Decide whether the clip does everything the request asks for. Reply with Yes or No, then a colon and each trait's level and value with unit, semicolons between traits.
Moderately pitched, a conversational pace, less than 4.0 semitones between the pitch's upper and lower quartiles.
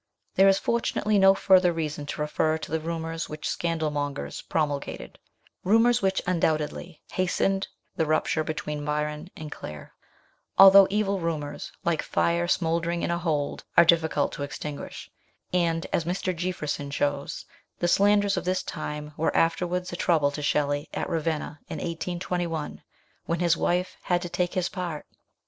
Yes: medium, 165 Hz; average, 155 wpm; average, 3.1 semitones